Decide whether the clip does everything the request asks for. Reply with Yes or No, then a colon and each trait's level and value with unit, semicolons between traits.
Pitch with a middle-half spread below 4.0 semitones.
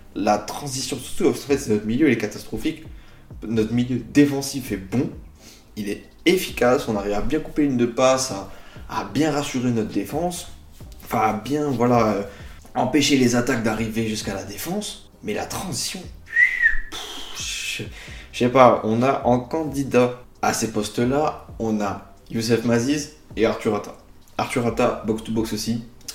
No: average, 4.5 semitones